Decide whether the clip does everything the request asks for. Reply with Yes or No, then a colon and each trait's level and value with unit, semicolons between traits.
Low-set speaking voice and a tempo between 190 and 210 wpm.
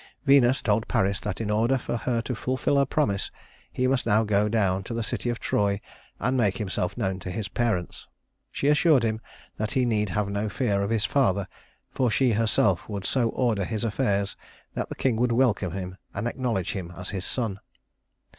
Yes: low, 110 Hz; average, 200 wpm